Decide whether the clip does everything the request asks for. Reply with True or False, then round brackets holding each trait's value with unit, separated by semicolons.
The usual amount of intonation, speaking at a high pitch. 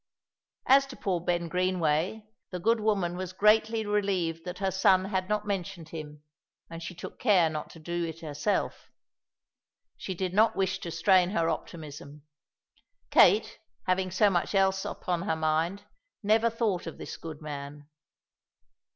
False (3.5 semitones; 180 Hz)